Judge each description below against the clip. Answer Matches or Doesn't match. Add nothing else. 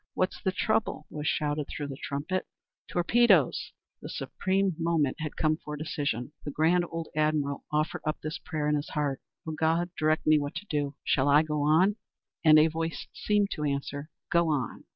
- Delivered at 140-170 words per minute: Doesn't match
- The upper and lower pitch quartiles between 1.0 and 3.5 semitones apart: Matches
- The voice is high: Doesn't match